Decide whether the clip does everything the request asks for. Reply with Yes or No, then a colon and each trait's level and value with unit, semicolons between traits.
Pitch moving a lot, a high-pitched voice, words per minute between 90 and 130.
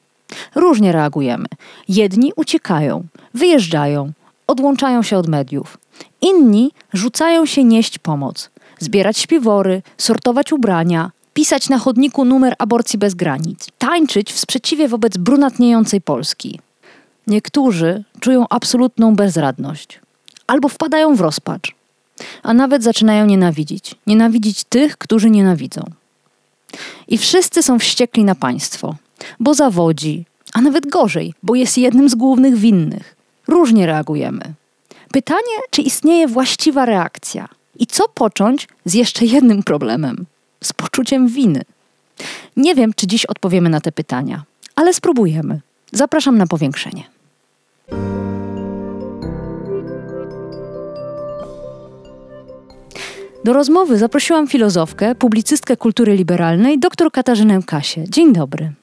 Yes: wide, 8.4 semitones; high, 225 Hz; slow, 110 wpm